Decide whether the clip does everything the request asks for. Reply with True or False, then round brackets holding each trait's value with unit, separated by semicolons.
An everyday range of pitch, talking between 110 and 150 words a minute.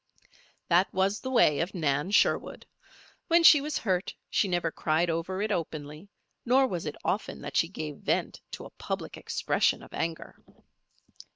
False (4.7 semitones; 165 wpm)